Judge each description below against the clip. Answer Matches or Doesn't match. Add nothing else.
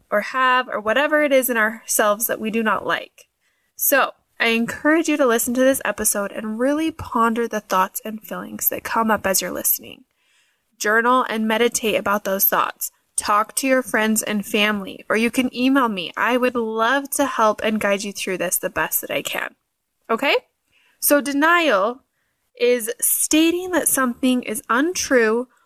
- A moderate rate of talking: Matches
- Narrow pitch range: Doesn't match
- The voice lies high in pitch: Matches